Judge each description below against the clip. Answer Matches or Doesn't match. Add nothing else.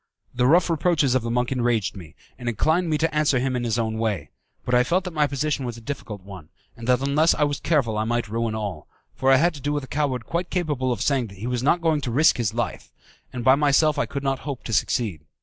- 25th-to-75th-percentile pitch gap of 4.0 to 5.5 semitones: Matches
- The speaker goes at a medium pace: Doesn't match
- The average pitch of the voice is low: Matches